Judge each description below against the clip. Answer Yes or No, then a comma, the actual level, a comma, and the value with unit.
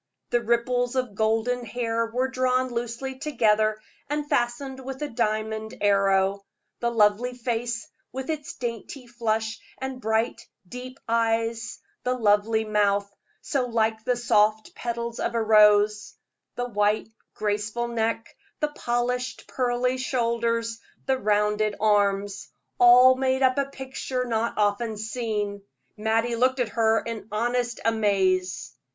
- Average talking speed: No, slow, 130 wpm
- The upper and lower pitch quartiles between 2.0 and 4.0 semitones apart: Yes, narrow, 2.6 semitones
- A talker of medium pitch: No, high, 230 Hz